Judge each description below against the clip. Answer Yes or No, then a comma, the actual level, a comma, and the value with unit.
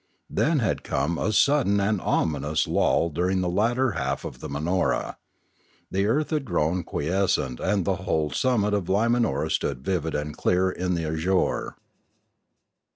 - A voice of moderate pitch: No, very low, 95 Hz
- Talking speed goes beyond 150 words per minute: Yes, average, 165 wpm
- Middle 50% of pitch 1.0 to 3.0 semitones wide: No, average, 4.8 semitones